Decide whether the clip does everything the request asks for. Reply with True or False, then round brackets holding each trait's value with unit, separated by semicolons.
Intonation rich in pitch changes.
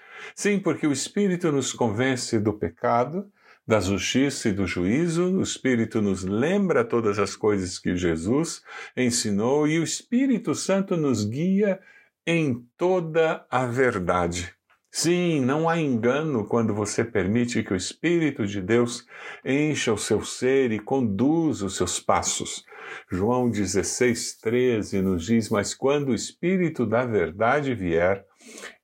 True (7.0 semitones)